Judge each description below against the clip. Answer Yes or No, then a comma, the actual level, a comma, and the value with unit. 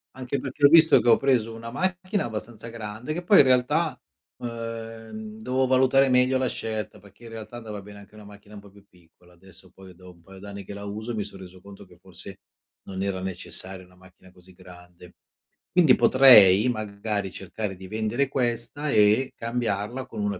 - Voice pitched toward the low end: Yes, low, 110 Hz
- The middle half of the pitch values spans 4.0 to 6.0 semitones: Yes, average, 4.6 semitones